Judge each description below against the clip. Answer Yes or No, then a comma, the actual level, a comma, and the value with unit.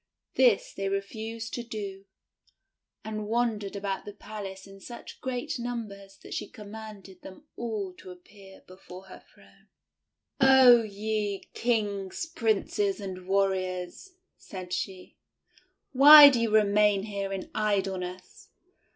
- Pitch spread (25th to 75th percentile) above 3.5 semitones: No, average, 2.7 semitones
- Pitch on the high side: Yes, high, 205 Hz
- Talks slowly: Yes, slow, 125 wpm